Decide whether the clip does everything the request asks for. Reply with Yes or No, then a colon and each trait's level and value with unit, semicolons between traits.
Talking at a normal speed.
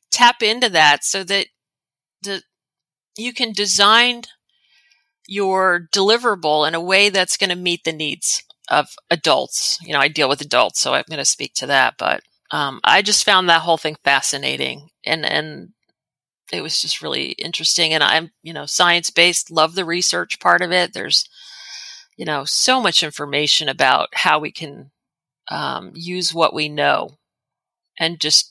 Yes: average, 170 wpm